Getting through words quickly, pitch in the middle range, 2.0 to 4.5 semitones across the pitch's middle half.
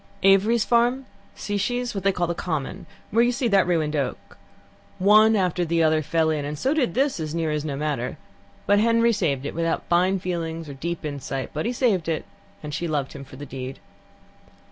No: fast, 215 wpm; medium, 170 Hz; wide, 5.6 semitones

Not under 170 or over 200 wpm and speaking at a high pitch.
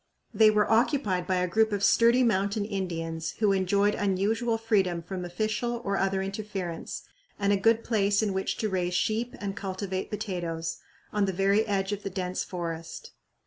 Yes: average, 175 wpm; high, 200 Hz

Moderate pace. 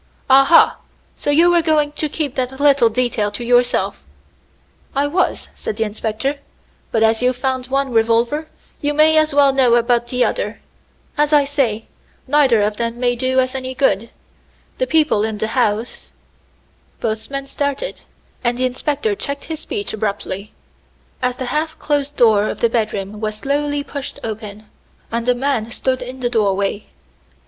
Yes: average, 170 wpm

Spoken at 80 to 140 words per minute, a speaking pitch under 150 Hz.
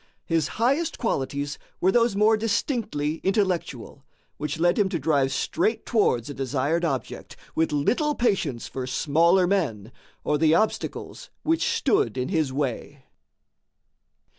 No: slow, 135 wpm; medium, 165 Hz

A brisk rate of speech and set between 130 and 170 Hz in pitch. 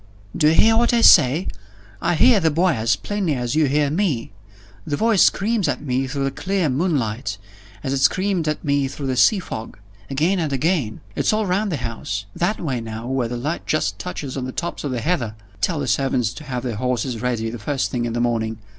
Yes: fast, 225 wpm; medium, 140 Hz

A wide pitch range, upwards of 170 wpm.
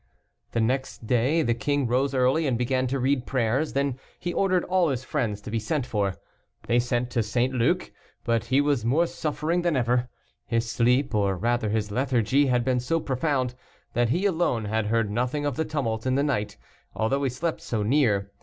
No: average, 3.6 semitones; average, 200 wpm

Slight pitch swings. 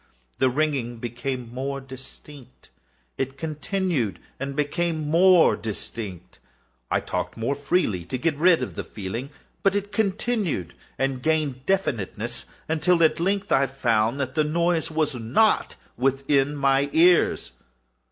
No: average, 4.9 semitones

